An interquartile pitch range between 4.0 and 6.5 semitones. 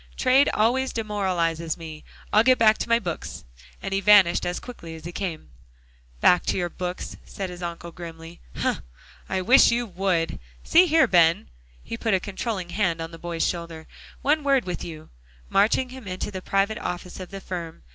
Yes: average, 4.4 semitones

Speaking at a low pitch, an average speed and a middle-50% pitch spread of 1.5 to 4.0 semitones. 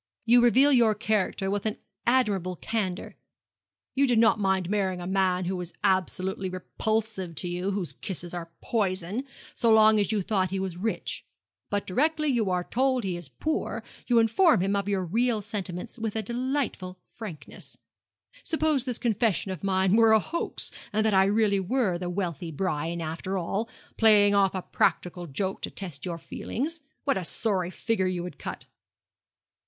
No: high, 195 Hz; average, 175 wpm; average, 3.7 semitones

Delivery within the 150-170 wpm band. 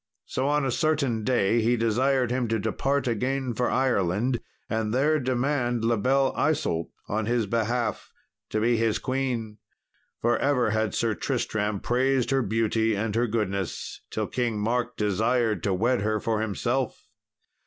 Yes: average, 155 wpm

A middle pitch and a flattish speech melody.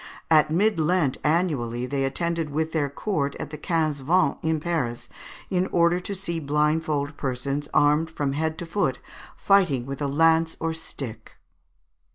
No: medium, 155 Hz; average, 3.0 semitones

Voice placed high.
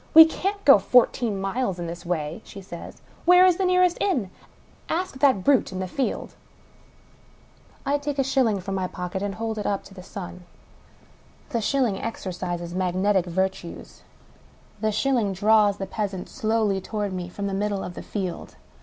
Yes: high, 205 Hz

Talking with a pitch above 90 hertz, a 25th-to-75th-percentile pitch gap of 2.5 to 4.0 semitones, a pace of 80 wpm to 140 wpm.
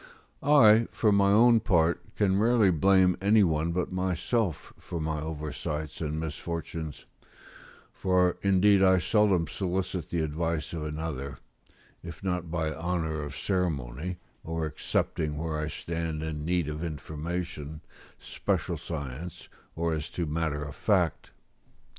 No: very low, 85 Hz; average, 3.2 semitones; slow, 135 wpm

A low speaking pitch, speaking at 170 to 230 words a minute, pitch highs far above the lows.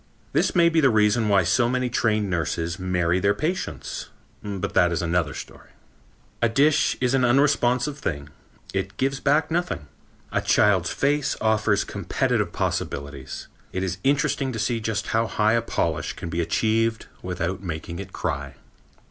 No: low, 105 Hz; average, 160 wpm; wide, 6.2 semitones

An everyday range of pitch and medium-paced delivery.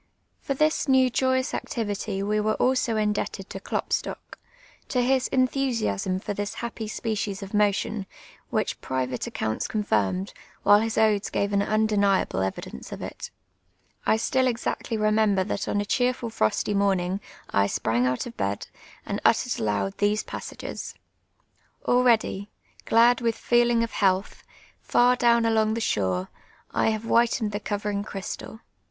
Yes: average, 3.2 semitones; average, 155 wpm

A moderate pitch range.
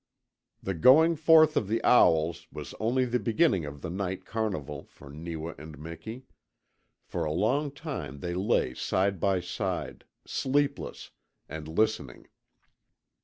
No: wide, 7.6 semitones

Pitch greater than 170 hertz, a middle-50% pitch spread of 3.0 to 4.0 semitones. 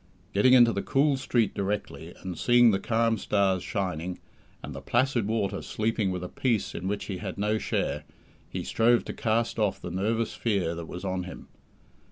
No: low, 105 Hz; average, 3.6 semitones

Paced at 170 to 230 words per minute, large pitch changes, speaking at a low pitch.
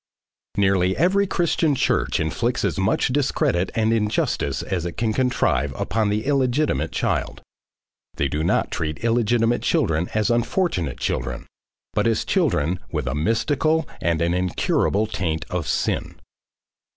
No: average, 140 wpm; wide, 6.8 semitones; low, 105 Hz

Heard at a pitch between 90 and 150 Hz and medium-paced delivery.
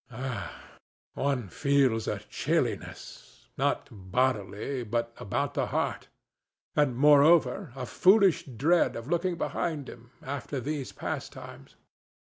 No: low, 135 Hz; slow, 100 wpm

